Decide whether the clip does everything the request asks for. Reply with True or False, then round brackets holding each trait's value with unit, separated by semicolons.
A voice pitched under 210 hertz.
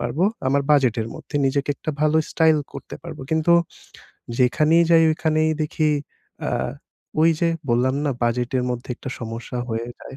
True (140 Hz)